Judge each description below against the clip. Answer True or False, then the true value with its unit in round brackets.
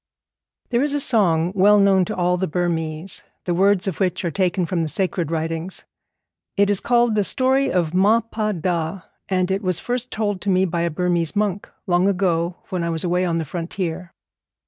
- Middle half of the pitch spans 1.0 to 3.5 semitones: True (3.0 semitones)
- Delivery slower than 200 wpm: False (205 wpm)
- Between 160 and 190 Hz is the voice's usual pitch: True (185 Hz)